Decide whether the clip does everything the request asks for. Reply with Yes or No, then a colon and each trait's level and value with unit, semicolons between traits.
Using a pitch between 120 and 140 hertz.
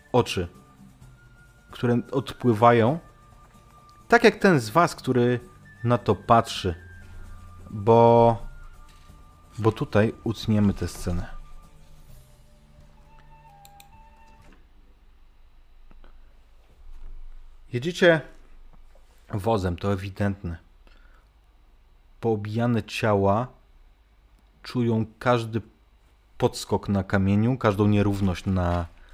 No: low, 100 Hz